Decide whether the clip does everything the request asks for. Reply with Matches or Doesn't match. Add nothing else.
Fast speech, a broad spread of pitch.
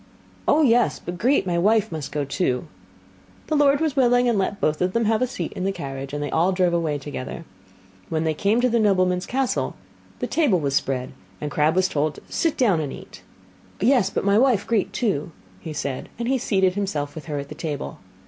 Matches